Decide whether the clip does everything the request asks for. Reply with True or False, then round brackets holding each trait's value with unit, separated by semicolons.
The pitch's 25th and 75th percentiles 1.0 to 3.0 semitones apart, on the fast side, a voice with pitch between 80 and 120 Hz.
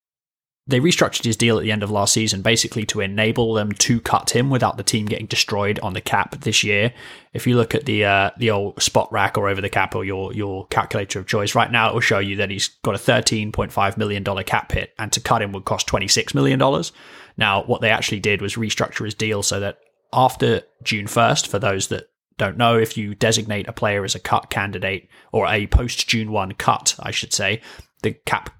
True (2.4 semitones; 235 wpm; 105 Hz)